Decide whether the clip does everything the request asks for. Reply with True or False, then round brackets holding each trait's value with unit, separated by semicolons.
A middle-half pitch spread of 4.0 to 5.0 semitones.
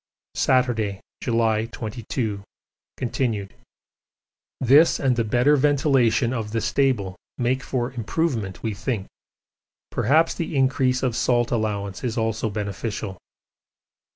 False (3.3 semitones)